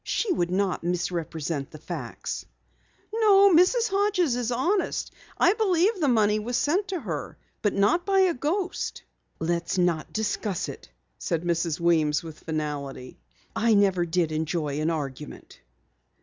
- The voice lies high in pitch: Yes, high, 195 Hz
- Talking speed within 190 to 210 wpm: No, average, 150 wpm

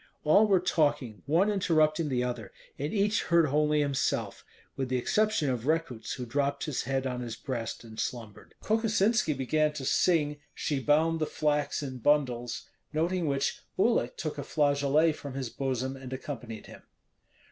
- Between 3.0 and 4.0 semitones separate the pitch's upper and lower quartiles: Yes, average, 3.7 semitones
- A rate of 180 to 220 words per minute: No, average, 165 wpm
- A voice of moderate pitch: Yes, medium, 145 Hz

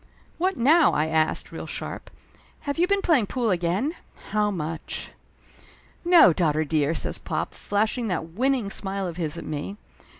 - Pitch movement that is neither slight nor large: No, wide, 8.4 semitones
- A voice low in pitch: No, high, 200 Hz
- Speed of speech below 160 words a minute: No, average, 165 wpm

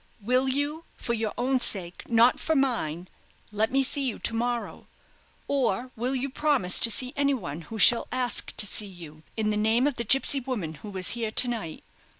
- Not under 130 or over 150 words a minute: No, average, 195 wpm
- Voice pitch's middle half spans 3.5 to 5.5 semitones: Yes, average, 4.0 semitones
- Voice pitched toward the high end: Yes, high, 235 Hz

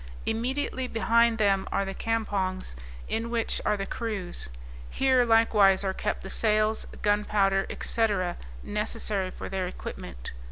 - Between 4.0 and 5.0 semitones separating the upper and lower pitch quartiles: No, average, 2.7 semitones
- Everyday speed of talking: No, slow, 130 wpm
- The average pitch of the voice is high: Yes, high, 210 Hz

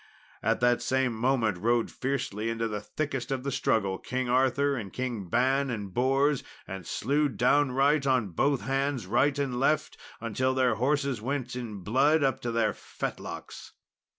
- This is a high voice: No, low, 130 Hz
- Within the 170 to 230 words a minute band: No, average, 160 wpm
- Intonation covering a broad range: No, average, 3.2 semitones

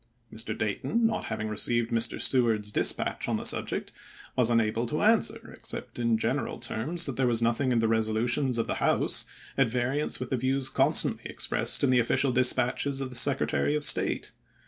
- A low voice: Yes, low, 120 Hz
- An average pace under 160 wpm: No, average, 185 wpm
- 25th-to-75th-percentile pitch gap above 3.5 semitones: No, average, 2.8 semitones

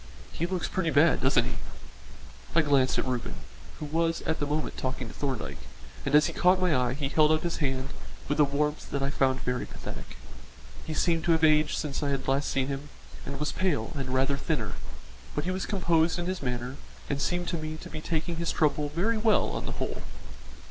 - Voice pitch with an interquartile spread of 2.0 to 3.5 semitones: Yes, average, 3.2 semitones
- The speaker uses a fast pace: Yes, fast, 215 wpm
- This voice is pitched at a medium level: Yes, medium, 150 Hz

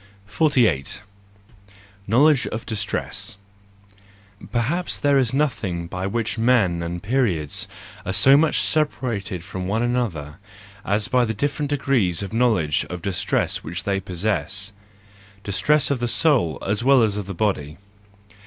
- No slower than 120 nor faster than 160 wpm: Yes, slow, 135 wpm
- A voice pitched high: No, low, 110 Hz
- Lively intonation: Yes, wide, 5.8 semitones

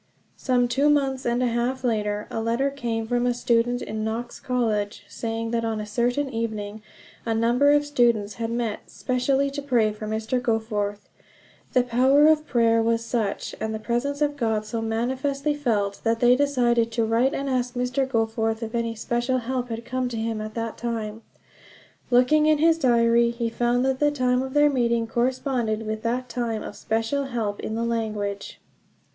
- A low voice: No, high, 235 Hz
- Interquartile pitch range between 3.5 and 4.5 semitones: No, narrow, 2.4 semitones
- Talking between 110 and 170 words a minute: No, average, 185 wpm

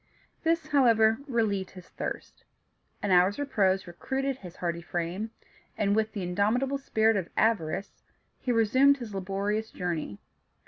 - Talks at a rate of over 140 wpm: No, slow, 135 wpm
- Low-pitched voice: No, high, 210 Hz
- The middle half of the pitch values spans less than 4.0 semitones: No, average, 4.3 semitones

